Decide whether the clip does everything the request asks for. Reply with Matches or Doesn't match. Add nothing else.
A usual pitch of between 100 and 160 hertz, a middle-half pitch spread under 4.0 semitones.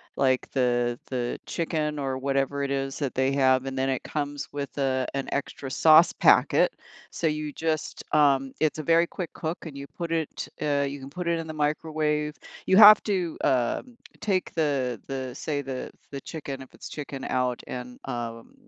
Matches